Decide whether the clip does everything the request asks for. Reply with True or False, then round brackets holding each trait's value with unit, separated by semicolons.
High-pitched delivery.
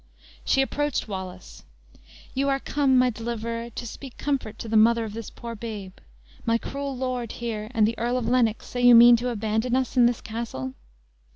True (235 Hz)